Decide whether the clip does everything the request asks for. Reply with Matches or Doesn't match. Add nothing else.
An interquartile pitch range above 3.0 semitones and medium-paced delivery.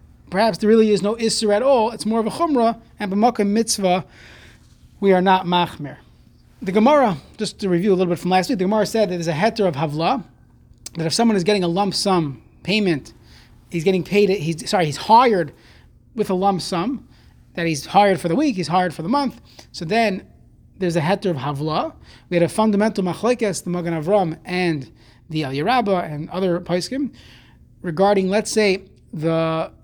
Matches